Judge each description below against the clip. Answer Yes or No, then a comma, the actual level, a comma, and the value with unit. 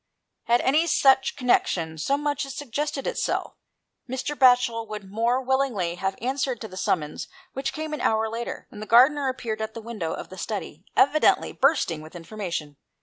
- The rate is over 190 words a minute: No, average, 175 wpm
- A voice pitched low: No, high, 235 Hz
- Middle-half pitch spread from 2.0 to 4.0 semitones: No, wide, 5.6 semitones